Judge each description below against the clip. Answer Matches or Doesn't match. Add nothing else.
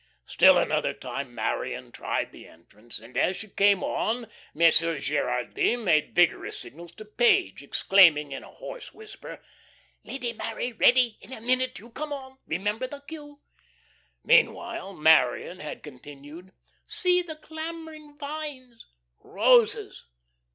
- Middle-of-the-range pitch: Doesn't match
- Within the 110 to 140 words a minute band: Matches